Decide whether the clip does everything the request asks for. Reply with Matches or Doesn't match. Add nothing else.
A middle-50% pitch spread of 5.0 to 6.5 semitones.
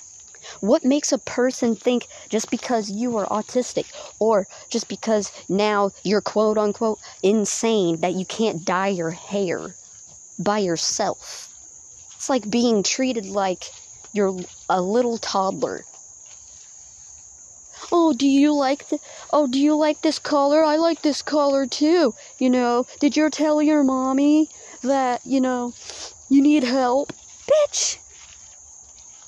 Matches